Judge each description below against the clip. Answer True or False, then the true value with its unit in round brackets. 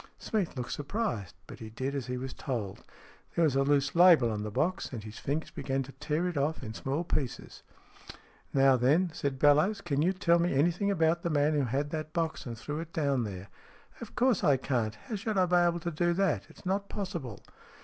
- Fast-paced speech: True (240 wpm)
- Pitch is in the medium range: True (150 Hz)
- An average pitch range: True (4.8 semitones)